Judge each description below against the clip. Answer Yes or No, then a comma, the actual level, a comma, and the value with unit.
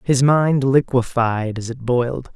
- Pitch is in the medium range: No, low, 125 Hz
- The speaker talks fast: No, average, 155 wpm